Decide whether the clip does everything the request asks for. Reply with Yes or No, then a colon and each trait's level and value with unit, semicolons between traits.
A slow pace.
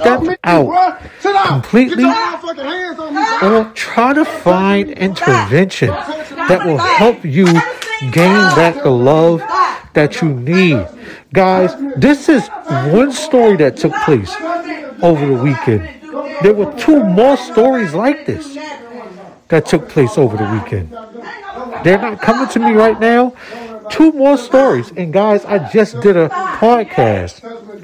Yes: slow, 130 wpm